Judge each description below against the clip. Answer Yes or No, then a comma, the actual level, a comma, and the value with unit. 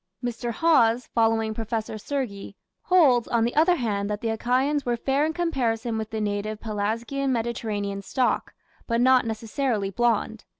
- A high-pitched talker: Yes, high, 230 Hz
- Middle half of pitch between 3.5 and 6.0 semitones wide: No, average, 3.0 semitones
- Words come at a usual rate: Yes, average, 155 wpm